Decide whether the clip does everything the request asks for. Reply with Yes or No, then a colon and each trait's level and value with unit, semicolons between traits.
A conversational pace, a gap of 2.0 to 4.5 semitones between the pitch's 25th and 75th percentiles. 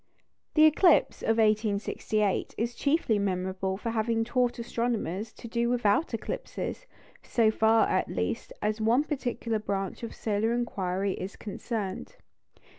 No: slow, 130 wpm; average, 2.8 semitones